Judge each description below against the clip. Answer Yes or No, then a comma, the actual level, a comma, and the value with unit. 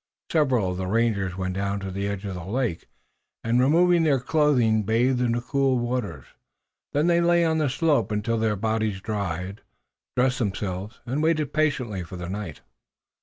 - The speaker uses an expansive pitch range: Yes, wide, 5.7 semitones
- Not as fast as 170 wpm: No, average, 175 wpm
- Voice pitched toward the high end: No, low, 115 Hz